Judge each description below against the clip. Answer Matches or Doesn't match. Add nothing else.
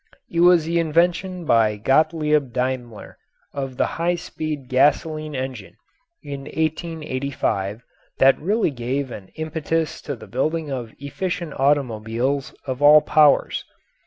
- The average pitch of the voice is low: Doesn't match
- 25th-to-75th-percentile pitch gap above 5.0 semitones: Doesn't match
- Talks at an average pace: Doesn't match